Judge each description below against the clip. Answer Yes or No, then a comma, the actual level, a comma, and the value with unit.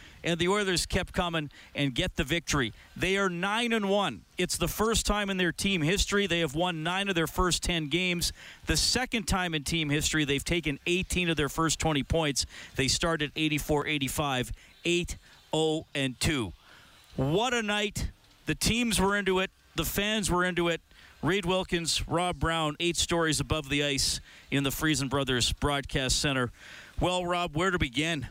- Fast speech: No, average, 175 wpm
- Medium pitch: Yes, medium, 165 Hz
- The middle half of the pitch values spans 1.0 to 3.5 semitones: No, average, 4.0 semitones